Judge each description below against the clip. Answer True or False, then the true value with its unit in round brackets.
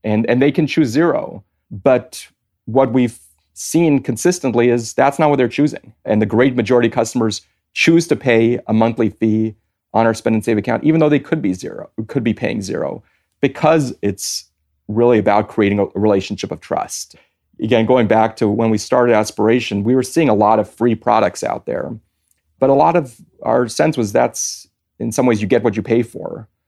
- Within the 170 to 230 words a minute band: True (200 wpm)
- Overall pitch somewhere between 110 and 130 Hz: True (115 Hz)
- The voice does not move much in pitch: False (3.4 semitones)